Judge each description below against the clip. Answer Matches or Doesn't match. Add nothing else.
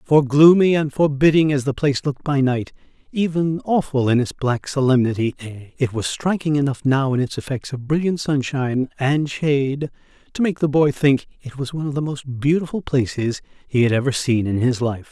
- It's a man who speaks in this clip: Matches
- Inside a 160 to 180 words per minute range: Doesn't match